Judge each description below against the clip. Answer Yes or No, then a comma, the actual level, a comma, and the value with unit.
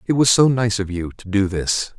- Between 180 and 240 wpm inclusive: No, fast, 275 wpm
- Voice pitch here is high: No, low, 110 Hz